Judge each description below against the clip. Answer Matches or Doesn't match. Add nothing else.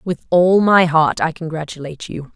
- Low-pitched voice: Doesn't match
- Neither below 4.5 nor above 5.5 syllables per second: Matches